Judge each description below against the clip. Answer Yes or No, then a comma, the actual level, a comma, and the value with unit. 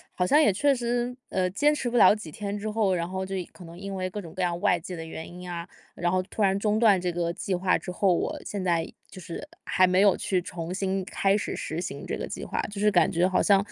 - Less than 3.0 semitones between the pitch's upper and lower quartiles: Yes, narrow, 2.6 semitones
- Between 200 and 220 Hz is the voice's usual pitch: No, high, 190 Hz